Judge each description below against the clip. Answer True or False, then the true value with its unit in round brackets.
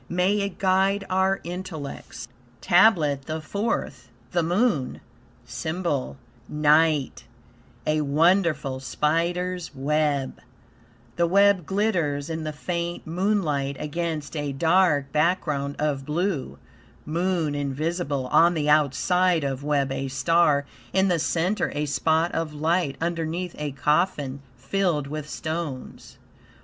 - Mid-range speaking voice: True (160 Hz)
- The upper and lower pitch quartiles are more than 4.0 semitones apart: False (3.7 semitones)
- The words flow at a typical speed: False (115 wpm)